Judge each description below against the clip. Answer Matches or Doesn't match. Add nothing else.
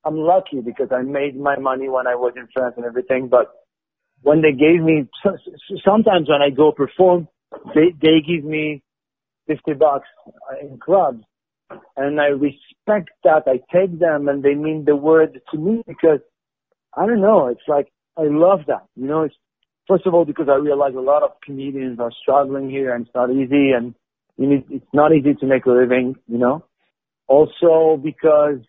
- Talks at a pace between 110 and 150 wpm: Doesn't match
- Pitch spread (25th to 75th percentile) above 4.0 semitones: Doesn't match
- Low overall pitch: Doesn't match